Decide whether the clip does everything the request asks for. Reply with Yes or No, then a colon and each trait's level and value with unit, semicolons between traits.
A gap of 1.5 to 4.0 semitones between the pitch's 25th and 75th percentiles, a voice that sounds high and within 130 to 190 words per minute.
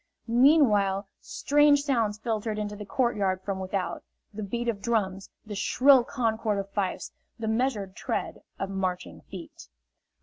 Yes: average, 3.4 semitones; high, 210 Hz; average, 140 wpm